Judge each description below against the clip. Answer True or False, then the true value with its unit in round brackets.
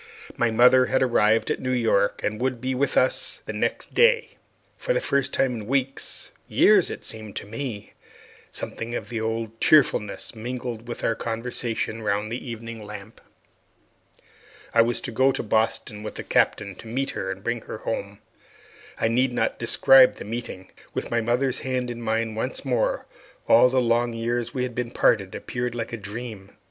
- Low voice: True (115 Hz)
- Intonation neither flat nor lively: False (2.3 semitones)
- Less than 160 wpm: False (180 wpm)